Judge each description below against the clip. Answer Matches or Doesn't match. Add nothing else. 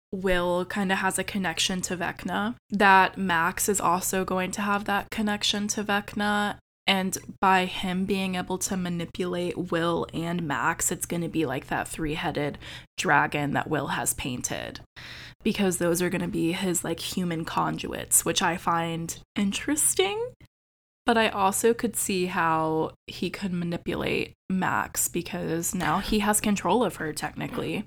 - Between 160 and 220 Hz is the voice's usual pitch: Matches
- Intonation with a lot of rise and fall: Doesn't match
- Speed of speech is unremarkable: Matches